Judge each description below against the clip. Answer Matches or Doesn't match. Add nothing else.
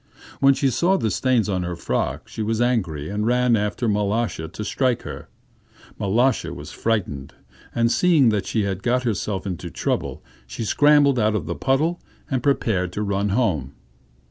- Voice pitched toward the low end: Matches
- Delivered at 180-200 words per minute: Doesn't match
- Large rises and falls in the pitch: Doesn't match